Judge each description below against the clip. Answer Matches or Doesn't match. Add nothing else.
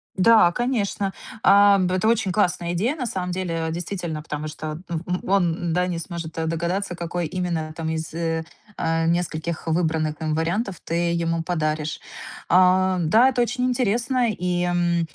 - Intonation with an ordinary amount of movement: Matches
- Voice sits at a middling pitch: Matches